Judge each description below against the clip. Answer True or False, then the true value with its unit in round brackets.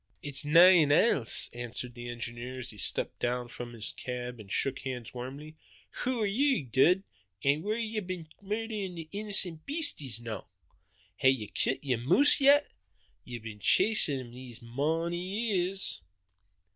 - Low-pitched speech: False (145 Hz)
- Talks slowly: False (160 wpm)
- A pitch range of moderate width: False (8.1 semitones)